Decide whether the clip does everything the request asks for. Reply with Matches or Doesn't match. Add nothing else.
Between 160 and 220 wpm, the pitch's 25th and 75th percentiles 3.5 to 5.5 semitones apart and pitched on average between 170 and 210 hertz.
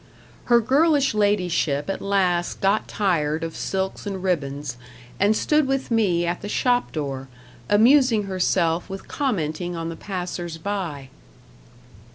Doesn't match